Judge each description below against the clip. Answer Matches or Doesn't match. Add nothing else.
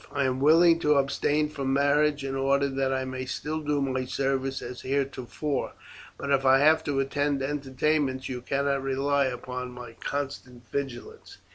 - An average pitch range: Doesn't match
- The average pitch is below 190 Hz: Matches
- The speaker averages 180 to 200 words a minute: Doesn't match